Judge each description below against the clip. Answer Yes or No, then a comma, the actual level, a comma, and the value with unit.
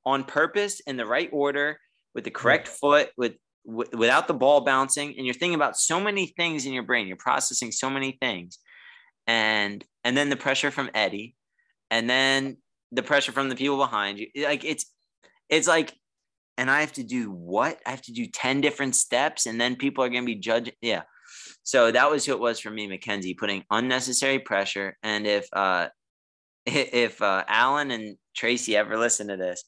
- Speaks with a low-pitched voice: Yes, low, 125 Hz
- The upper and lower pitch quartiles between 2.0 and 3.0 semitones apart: No, average, 4.5 semitones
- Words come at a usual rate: Yes, average, 195 wpm